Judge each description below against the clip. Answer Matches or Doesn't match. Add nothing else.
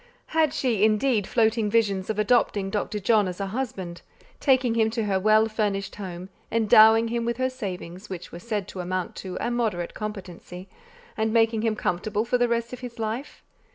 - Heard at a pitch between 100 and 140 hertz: Doesn't match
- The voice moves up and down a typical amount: Matches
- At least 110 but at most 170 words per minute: Doesn't match